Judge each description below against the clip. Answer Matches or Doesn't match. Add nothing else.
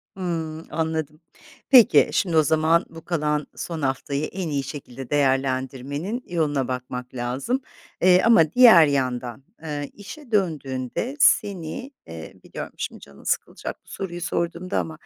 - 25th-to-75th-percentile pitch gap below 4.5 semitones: Doesn't match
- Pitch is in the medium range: Matches